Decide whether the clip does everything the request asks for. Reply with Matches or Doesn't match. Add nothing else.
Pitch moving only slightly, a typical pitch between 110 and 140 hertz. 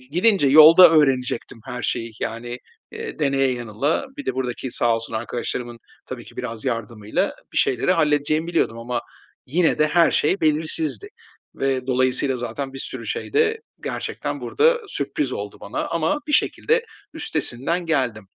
Doesn't match